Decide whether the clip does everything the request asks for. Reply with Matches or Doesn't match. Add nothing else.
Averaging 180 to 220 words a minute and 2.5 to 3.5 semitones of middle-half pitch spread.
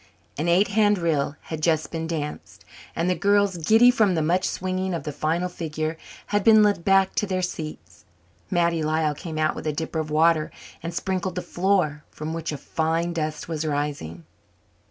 Matches